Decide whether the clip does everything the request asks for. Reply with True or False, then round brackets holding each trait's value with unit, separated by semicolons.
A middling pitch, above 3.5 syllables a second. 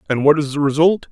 True (150 Hz; 6.6 syllables/s)